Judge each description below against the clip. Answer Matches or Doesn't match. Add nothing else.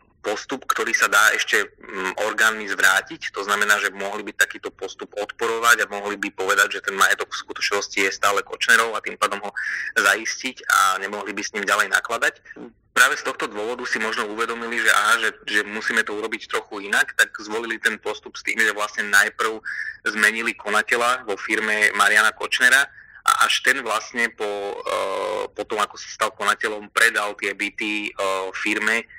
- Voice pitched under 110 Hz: Doesn't match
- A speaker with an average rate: Doesn't match